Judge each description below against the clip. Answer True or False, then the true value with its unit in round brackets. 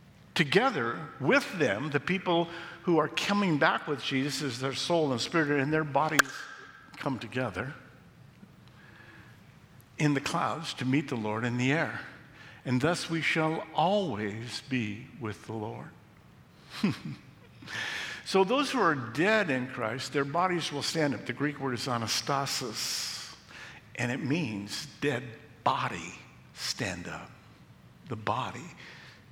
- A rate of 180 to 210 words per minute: False (135 wpm)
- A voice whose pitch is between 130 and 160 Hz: True (140 Hz)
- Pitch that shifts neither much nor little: True (4.6 semitones)